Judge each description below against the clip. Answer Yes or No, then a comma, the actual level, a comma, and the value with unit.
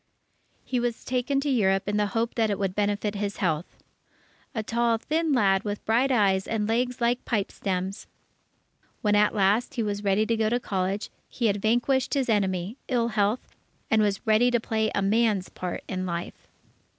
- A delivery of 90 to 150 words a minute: No, average, 185 wpm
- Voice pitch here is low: No, high, 215 Hz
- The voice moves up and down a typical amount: Yes, average, 3.1 semitones